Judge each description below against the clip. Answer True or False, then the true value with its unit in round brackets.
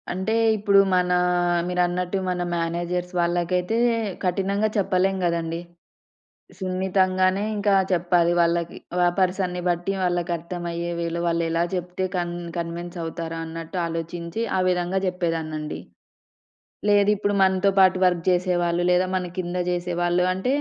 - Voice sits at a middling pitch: True (180 Hz)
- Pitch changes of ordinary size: False (1.5 semitones)